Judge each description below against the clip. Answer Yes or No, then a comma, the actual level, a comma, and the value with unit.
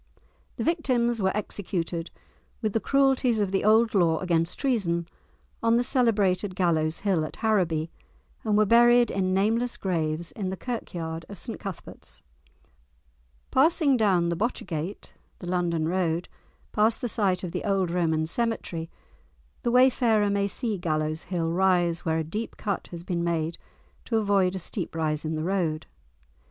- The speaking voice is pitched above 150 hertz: Yes, high, 190 Hz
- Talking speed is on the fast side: No, average, 155 wpm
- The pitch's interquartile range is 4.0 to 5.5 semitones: Yes, average, 4.8 semitones